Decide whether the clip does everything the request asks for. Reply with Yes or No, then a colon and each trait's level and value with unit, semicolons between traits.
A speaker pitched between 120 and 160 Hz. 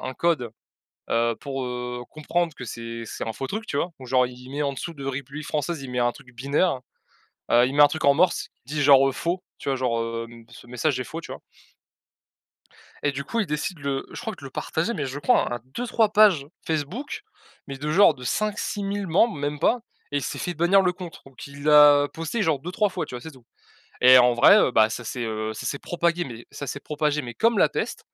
Yes: medium, 140 Hz